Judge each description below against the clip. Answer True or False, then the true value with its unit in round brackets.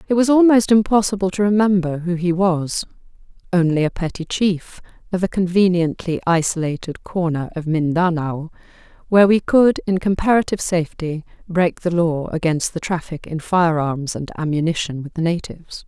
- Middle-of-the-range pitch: True (175 Hz)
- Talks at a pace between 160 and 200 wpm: False (145 wpm)